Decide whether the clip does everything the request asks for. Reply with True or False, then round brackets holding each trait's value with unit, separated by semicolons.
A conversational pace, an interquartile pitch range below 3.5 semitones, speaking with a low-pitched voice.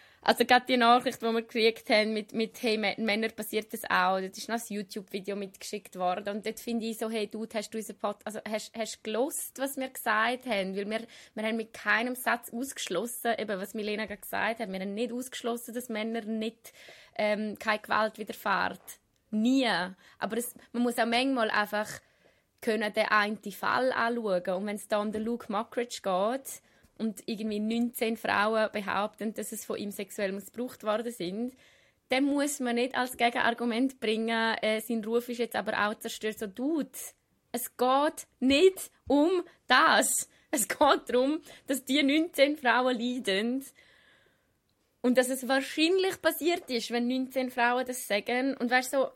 False (175 wpm; 2.7 semitones; 230 Hz)